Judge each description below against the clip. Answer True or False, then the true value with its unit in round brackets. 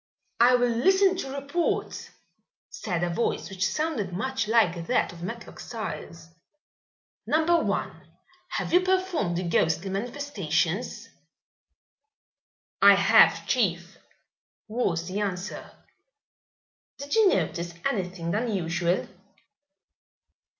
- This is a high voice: True (210 Hz)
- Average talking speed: False (100 wpm)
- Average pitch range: False (8.0 semitones)